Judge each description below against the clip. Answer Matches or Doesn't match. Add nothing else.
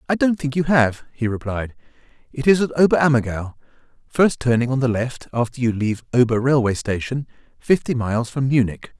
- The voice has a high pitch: Doesn't match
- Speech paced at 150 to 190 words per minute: Matches